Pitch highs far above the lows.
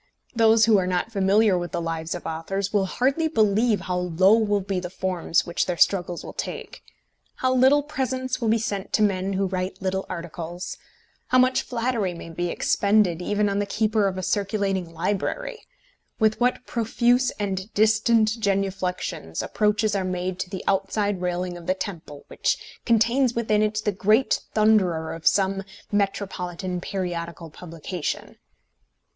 No: average, 3.3 semitones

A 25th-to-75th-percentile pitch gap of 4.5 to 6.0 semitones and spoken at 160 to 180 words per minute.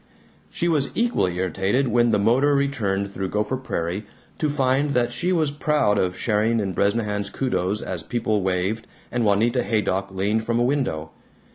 Yes: average, 5.1 semitones; average, 165 wpm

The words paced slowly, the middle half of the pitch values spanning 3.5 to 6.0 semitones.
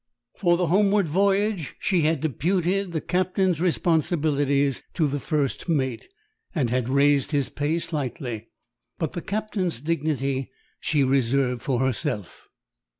Yes: slow, 130 wpm; average, 4.5 semitones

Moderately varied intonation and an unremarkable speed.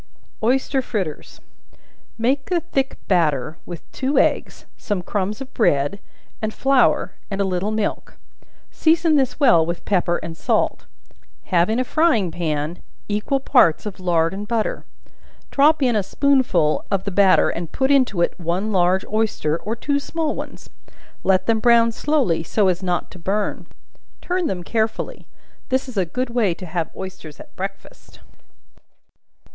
No: wide, 6.6 semitones; average, 155 wpm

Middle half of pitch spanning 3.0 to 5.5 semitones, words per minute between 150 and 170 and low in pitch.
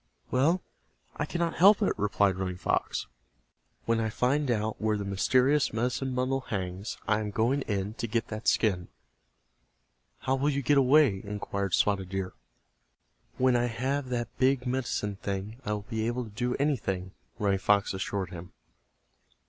Yes: average, 4.5 semitones; average, 160 wpm; low, 115 Hz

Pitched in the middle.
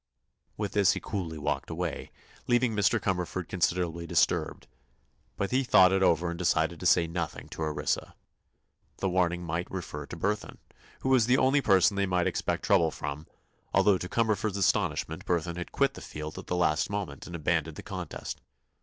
No: very low, 90 Hz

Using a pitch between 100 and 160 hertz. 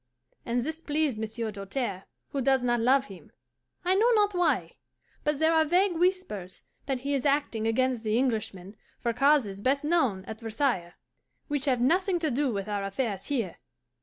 No: very high, 255 Hz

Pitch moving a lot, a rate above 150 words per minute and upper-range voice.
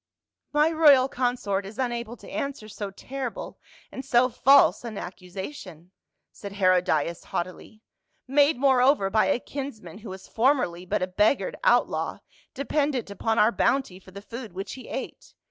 Yes: wide, 5.8 semitones; average, 160 wpm; high, 230 Hz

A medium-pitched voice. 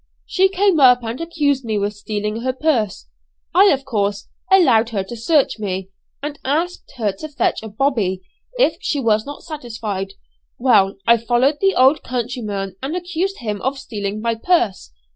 No: high, 240 Hz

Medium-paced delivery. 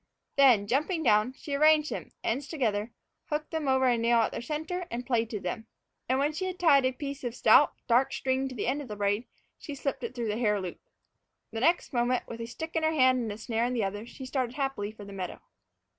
No: fast, 240 wpm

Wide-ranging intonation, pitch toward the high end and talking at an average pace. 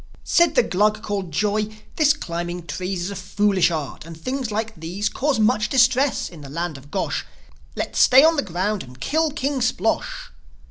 Yes: wide, 6.7 semitones; high, 205 Hz; average, 185 wpm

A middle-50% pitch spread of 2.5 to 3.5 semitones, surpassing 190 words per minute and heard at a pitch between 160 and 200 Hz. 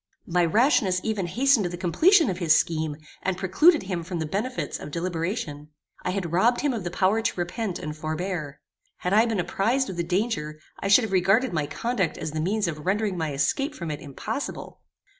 No: average, 5.0 semitones; average, 200 wpm; medium, 185 Hz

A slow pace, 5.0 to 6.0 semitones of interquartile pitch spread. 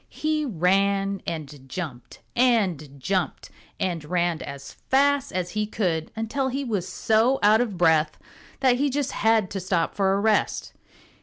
No: average, 155 wpm; wide, 5.6 semitones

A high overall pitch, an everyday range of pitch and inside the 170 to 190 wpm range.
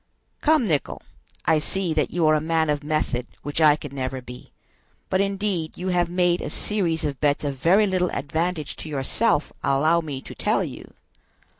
No: medium, 160 Hz; average, 3.7 semitones; average, 185 wpm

